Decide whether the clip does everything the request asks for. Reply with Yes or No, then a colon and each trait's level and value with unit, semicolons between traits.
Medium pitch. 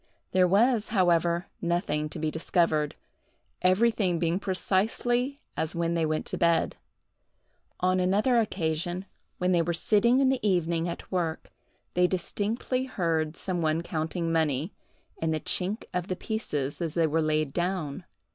Yes: medium, 175 Hz